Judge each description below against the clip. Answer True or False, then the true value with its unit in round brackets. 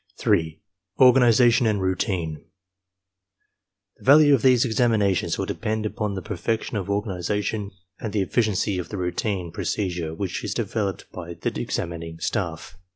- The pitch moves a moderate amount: True (3.9 semitones)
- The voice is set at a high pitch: False (100 Hz)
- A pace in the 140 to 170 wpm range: True (150 wpm)